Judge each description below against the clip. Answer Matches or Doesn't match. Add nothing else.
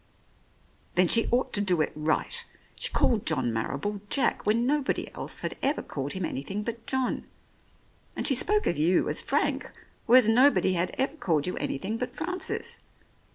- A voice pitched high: Matches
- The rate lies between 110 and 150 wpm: Doesn't match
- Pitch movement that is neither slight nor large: Doesn't match